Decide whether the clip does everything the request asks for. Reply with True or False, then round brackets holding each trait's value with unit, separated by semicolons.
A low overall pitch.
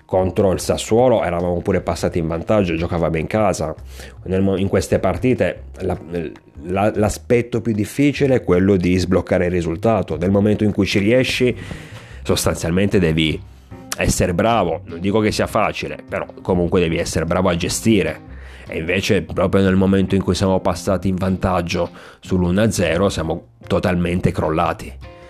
True (95 Hz)